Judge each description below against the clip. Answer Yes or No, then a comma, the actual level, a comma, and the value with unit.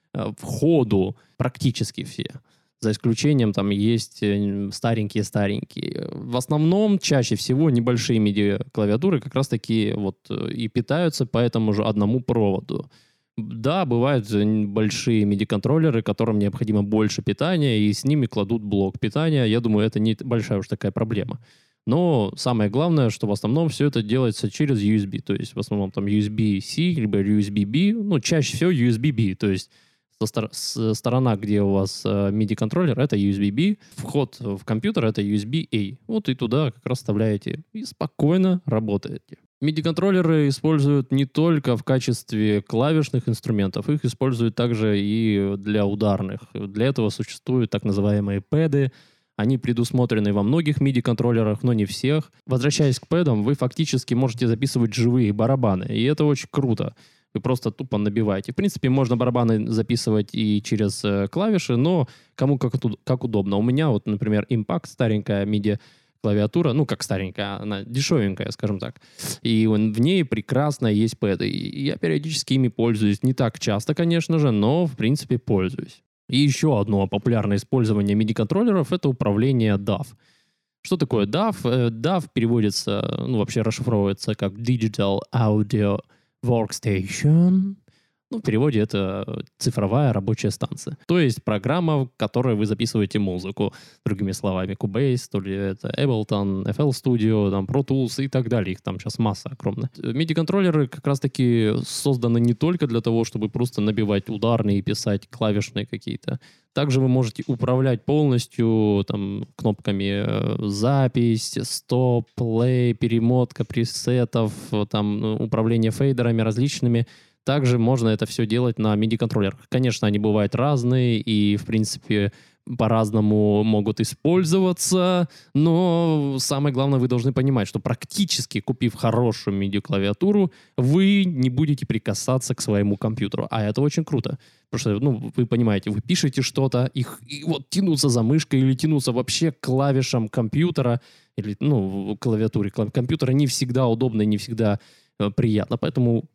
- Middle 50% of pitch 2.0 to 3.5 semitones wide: No, average, 4.7 semitones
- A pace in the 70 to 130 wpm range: No, average, 140 wpm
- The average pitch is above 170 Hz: No, low, 120 Hz